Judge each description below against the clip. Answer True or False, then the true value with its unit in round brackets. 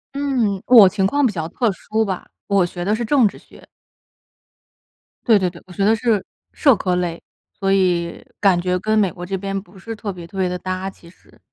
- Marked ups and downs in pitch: False (3.1 semitones)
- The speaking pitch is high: True (195 Hz)